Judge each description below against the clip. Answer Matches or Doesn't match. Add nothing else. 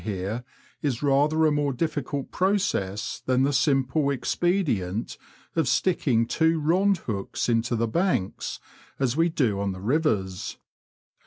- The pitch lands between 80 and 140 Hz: Matches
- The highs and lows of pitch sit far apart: Matches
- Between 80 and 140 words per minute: Matches